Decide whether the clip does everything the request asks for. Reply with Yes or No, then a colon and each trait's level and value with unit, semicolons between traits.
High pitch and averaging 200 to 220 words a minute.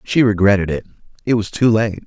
No: low, 105 Hz; fast, 205 wpm